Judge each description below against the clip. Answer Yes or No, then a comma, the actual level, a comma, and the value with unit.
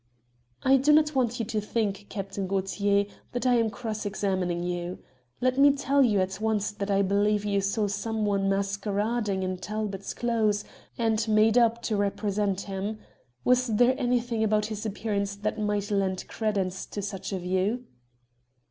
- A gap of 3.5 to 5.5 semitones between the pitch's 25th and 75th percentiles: No, narrow, 2.5 semitones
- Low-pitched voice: No, high, 210 Hz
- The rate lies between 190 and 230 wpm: No, average, 165 wpm